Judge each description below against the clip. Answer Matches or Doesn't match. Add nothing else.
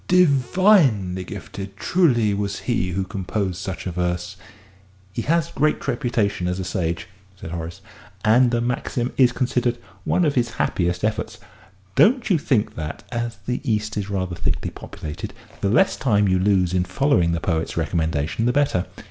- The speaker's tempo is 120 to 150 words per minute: Doesn't match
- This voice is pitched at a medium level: Doesn't match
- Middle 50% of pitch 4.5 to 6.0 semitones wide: Matches